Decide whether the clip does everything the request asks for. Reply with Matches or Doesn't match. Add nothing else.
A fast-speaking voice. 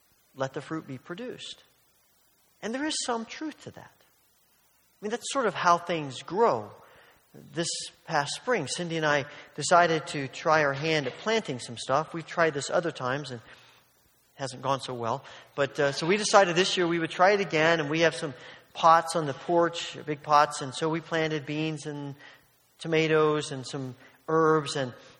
Doesn't match